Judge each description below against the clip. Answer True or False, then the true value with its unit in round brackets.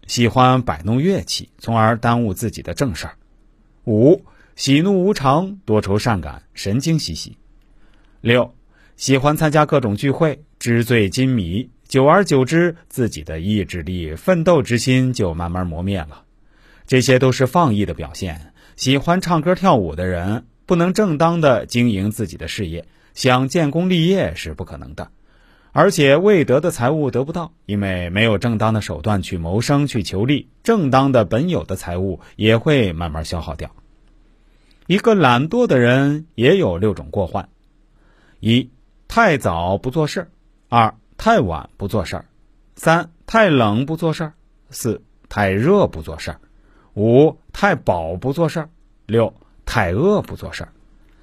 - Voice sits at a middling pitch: False (120 Hz)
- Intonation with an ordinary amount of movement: False (7.6 semitones)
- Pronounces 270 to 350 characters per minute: False (220 characters per minute)